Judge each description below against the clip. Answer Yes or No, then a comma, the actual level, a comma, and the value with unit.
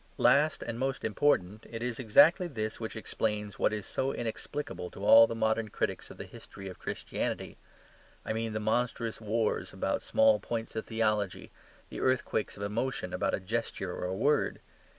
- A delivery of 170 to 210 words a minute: Yes, average, 175 wpm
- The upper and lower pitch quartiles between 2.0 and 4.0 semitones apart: Yes, average, 2.8 semitones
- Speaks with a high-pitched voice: No, low, 110 Hz